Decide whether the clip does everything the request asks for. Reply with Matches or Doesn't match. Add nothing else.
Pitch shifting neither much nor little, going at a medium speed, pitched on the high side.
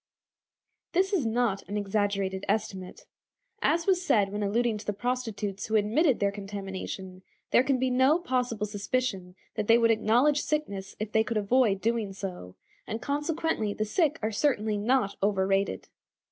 Matches